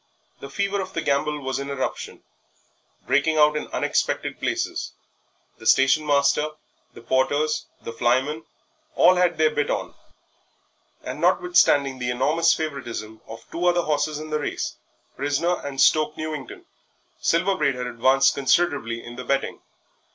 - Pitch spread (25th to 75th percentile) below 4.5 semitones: Yes, average, 2.9 semitones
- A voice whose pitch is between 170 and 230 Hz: No, medium, 145 Hz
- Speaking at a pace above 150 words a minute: No, average, 145 wpm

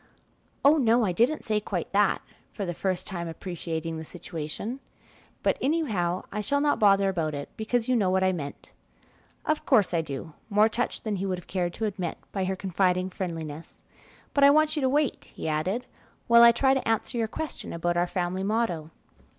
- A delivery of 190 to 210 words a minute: Yes, average, 200 wpm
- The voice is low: No, high, 195 Hz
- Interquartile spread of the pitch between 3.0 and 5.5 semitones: Yes, average, 5.2 semitones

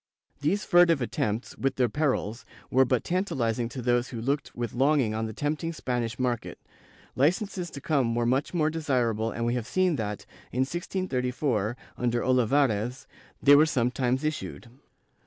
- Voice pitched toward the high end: No, low, 130 Hz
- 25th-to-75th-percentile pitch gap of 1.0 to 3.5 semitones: No, average, 4.1 semitones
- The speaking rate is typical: Yes, average, 160 wpm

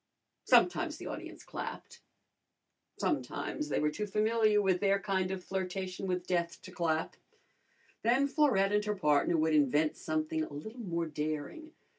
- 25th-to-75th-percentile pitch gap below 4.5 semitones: No, average, 4.9 semitones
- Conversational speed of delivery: Yes, average, 150 wpm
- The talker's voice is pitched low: No, medium, 185 Hz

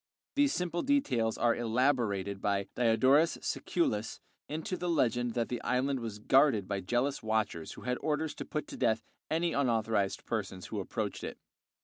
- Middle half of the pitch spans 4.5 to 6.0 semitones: Yes, average, 5.2 semitones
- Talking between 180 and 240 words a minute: No, average, 160 wpm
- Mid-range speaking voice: No, low, 120 Hz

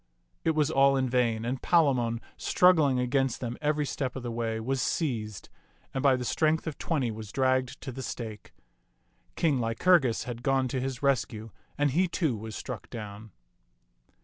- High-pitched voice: No, low, 130 Hz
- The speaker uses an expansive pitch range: No, average, 3.4 semitones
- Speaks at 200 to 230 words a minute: No, average, 175 wpm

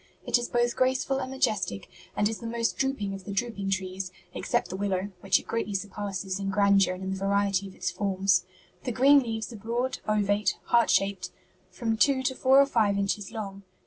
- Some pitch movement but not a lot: Yes, average, 3.4 semitones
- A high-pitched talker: Yes, high, 205 Hz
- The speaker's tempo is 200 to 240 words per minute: Yes, fast, 205 wpm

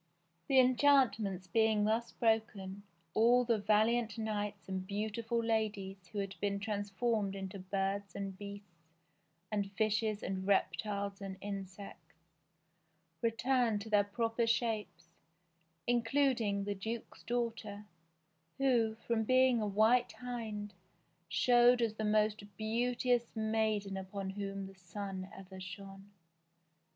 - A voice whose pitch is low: No, high, 210 Hz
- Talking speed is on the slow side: Yes, slow, 120 wpm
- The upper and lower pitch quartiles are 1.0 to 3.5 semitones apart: Yes, narrow, 2.6 semitones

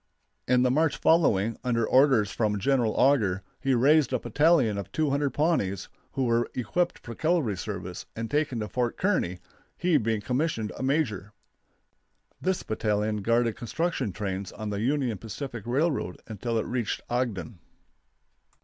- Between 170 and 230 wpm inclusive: No, average, 150 wpm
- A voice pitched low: Yes, low, 120 Hz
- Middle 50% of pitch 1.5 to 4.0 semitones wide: No, average, 5.1 semitones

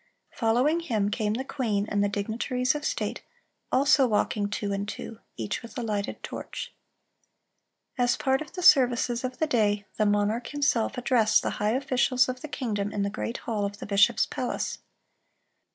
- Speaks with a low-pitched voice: No, high, 230 Hz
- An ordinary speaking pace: Yes, average, 180 wpm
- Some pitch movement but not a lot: Yes, average, 3.8 semitones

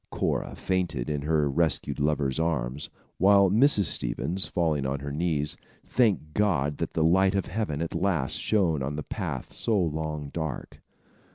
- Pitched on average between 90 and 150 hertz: No, very low, 80 Hz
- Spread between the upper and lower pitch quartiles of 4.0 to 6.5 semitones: Yes, average, 4.5 semitones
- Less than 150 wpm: No, average, 160 wpm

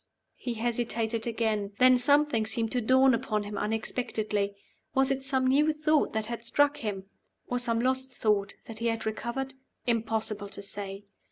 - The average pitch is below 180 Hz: No, high, 230 Hz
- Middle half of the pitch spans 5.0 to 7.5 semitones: No, average, 3.3 semitones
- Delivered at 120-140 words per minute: No, average, 165 wpm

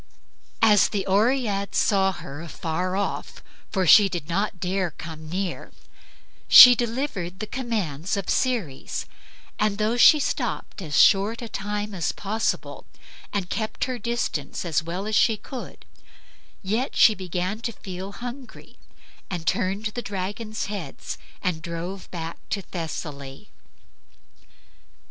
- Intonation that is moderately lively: Yes, average, 3.8 semitones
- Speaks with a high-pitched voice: Yes, high, 195 Hz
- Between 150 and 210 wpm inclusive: No, slow, 135 wpm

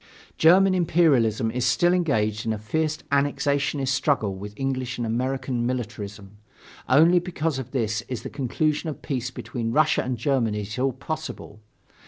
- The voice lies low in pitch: Yes, low, 130 Hz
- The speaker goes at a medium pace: Yes, average, 155 wpm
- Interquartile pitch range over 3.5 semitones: Yes, average, 5.0 semitones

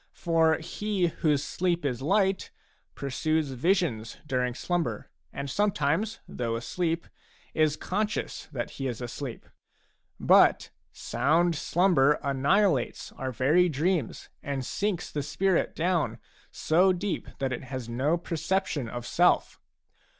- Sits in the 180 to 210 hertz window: No, medium, 155 Hz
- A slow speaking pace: Yes, slow, 120 wpm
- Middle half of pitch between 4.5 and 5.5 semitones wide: Yes, average, 5.1 semitones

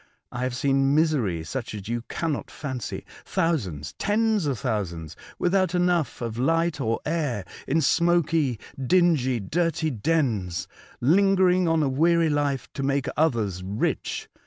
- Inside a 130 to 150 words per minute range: Yes, average, 140 wpm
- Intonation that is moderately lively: No, wide, 6.0 semitones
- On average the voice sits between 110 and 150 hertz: Yes, medium, 140 Hz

